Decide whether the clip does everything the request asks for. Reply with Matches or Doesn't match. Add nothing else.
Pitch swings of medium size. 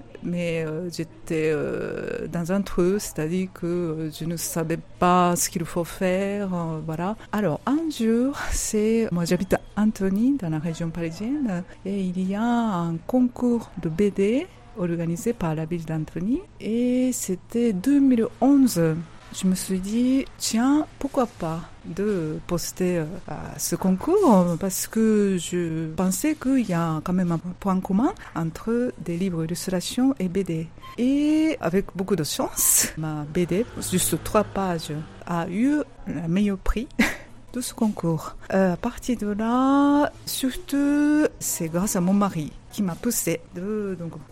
Doesn't match